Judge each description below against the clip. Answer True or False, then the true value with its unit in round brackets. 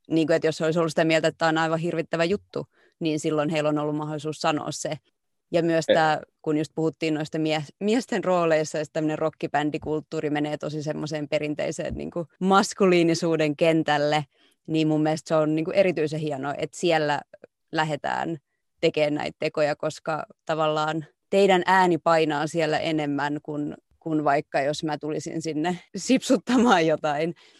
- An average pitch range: False (1.4 semitones)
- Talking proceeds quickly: True (160 wpm)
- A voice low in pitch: False (155 Hz)